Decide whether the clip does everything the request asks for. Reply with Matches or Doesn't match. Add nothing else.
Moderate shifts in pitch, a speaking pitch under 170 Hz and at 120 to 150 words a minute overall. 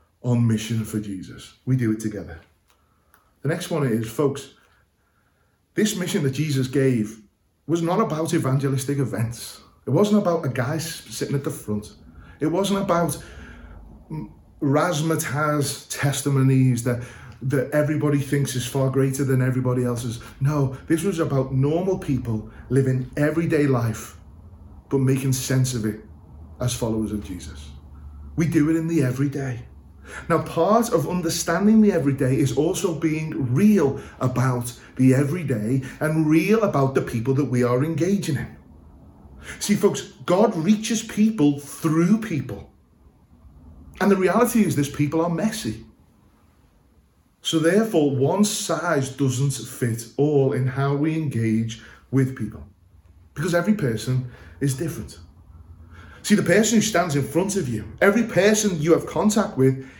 Doesn't match